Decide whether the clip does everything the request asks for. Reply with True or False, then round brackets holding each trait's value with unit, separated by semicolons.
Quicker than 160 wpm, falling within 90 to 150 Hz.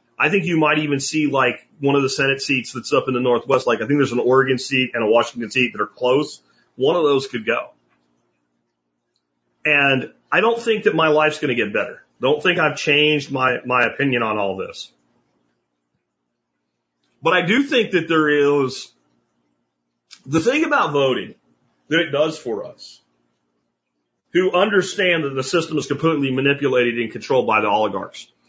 True (180 wpm; 135 Hz)